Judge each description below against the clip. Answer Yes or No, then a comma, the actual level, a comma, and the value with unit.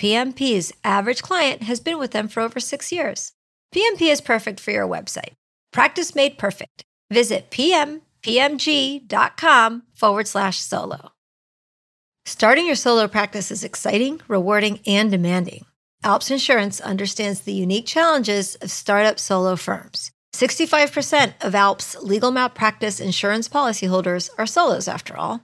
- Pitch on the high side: Yes, high, 220 Hz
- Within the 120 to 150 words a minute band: Yes, slow, 135 wpm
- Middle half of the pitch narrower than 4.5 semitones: No, wide, 5.5 semitones